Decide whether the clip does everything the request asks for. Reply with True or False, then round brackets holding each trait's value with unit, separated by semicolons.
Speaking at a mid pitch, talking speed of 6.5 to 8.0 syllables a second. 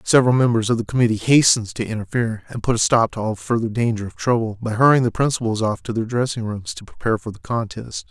False (115 Hz; 6.6 syllables/s)